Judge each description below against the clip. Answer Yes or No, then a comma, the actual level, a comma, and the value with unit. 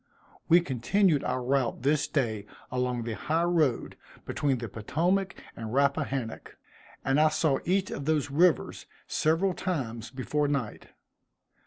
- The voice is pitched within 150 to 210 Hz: No, medium, 140 Hz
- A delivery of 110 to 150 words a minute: Yes, slow, 135 wpm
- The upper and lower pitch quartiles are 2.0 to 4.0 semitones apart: No, average, 4.4 semitones